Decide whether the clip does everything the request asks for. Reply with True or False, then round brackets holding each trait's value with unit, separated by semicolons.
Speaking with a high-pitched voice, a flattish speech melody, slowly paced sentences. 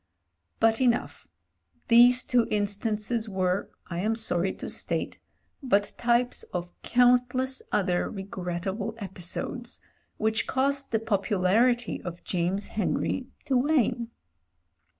False (220 Hz; 4.3 semitones; 110 wpm)